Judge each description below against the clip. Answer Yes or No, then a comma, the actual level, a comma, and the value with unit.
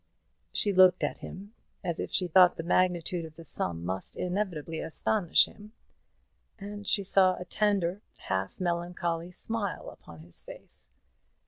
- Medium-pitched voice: Yes, medium, 180 Hz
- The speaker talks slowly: No, average, 145 wpm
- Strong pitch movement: No, average, 3.1 semitones